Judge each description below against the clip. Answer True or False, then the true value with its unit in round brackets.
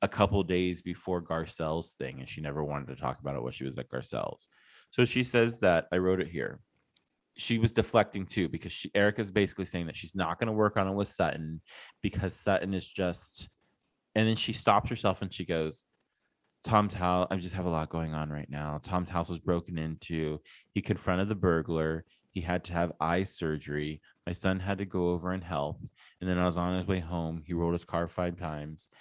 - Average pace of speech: False (225 wpm)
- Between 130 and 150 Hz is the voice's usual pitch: False (90 Hz)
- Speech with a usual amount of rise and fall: True (3.2 semitones)